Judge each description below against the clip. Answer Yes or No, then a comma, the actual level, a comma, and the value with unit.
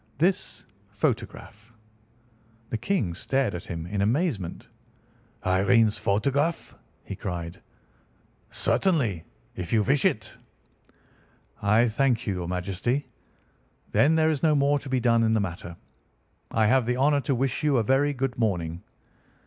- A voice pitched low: Yes, low, 115 Hz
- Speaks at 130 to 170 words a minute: Yes, slow, 135 wpm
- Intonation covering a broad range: Yes, wide, 5.9 semitones